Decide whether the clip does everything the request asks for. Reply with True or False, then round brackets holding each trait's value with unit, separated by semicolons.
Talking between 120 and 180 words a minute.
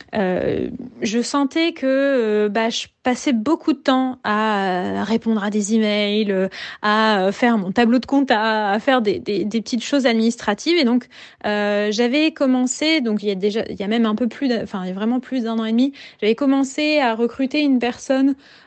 False (205 wpm)